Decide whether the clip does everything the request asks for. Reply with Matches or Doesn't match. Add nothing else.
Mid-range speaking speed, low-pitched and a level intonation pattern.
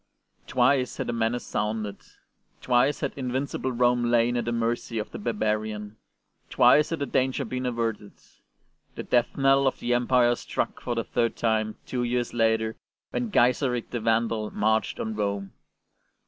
Matches